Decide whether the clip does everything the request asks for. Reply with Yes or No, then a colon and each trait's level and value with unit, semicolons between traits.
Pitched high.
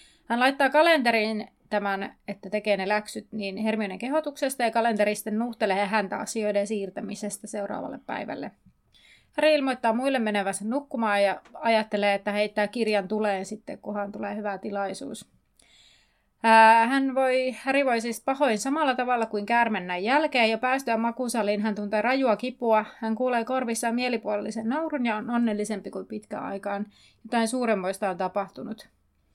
Yes: high, 220 Hz